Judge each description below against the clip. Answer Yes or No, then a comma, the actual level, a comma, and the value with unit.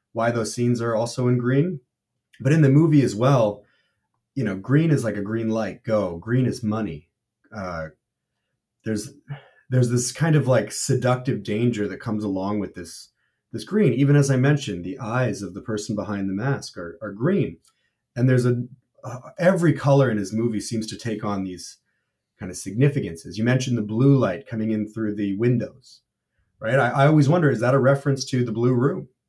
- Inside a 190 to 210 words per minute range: Yes, average, 195 wpm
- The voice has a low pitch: Yes, low, 120 Hz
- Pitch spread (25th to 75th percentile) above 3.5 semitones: Yes, average, 4.5 semitones